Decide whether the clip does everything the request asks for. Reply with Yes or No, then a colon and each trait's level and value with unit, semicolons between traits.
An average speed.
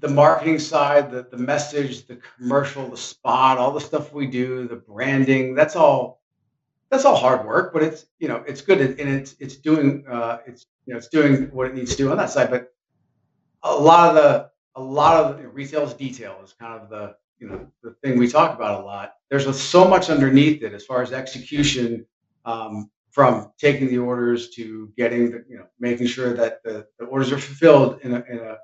No: fast, 215 wpm